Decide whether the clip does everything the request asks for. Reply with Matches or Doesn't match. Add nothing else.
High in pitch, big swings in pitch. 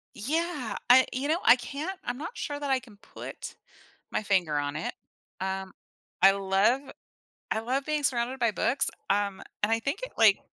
Matches